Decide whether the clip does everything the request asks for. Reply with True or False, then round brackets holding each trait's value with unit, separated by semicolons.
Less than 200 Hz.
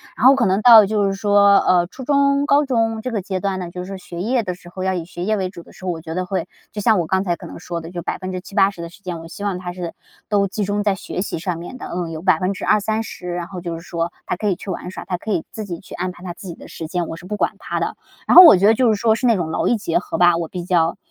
True (185 Hz)